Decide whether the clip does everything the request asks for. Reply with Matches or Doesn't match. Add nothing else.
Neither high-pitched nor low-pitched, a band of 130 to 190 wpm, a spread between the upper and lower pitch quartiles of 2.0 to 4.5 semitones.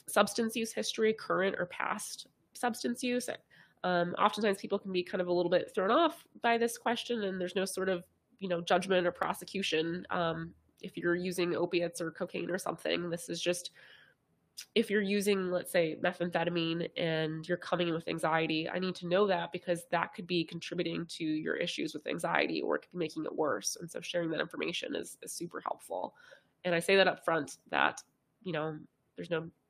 Doesn't match